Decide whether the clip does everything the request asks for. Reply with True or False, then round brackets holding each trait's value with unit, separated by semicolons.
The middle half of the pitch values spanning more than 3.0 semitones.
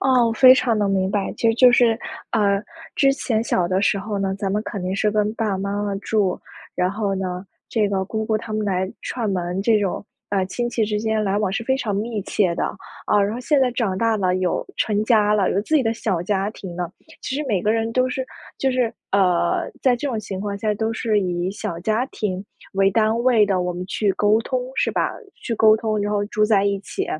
False (2.7 semitones)